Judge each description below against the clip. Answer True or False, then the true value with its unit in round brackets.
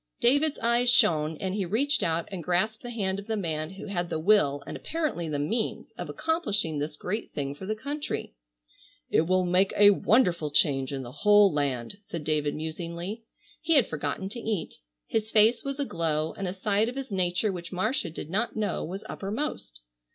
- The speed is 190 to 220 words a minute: True (195 wpm)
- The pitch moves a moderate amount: False (5.7 semitones)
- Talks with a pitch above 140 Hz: True (190 Hz)